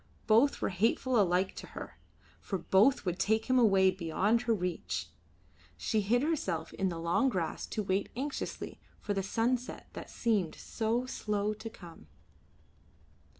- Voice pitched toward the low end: No, high, 210 Hz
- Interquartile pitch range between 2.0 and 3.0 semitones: No, average, 4.0 semitones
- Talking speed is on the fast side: No, average, 150 wpm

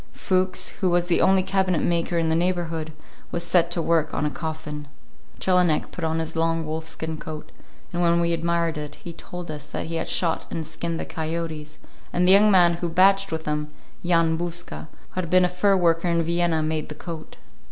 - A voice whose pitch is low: No, medium, 170 Hz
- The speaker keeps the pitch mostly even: Yes, narrow, 1.7 semitones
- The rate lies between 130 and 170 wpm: No, fast, 205 wpm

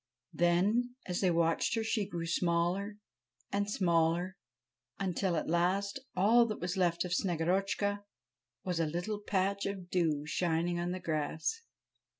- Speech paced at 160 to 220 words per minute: No, average, 145 wpm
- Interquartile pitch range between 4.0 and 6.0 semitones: No, average, 2.8 semitones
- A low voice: No, medium, 180 Hz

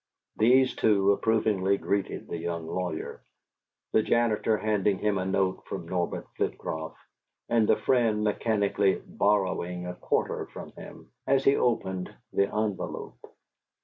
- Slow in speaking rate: Yes, slow, 130 wpm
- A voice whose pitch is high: No, low, 100 Hz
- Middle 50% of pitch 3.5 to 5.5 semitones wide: No, average, 2.9 semitones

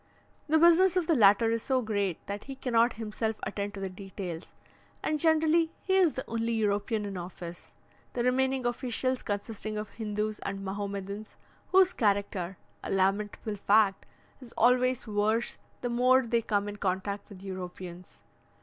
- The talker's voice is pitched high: Yes, high, 215 Hz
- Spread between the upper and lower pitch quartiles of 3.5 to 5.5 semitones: Yes, average, 4.0 semitones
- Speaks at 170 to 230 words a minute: No, average, 160 wpm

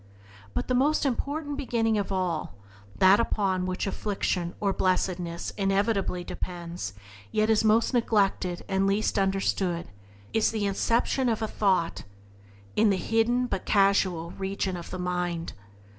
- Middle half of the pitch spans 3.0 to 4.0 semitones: Yes, average, 3.7 semitones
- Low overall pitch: No, high, 195 Hz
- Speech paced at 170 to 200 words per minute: No, average, 145 wpm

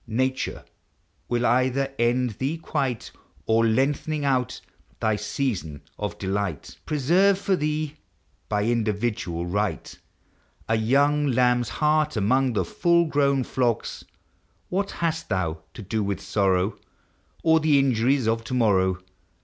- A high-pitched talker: No, low, 125 Hz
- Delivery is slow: Yes, slow, 130 wpm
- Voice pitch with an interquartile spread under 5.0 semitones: No, average, 5.3 semitones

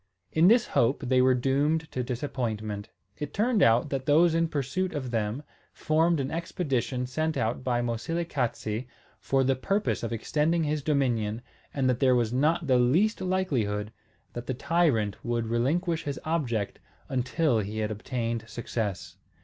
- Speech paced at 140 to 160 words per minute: Yes, average, 155 wpm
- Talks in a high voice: No, low, 130 Hz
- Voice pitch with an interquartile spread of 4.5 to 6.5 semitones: Yes, average, 5.2 semitones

